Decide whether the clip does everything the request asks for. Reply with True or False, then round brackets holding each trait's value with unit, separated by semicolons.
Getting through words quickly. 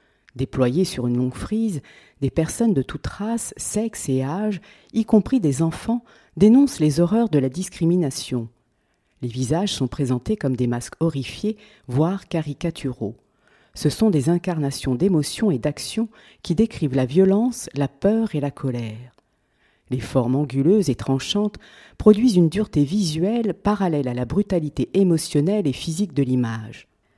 False (150 wpm)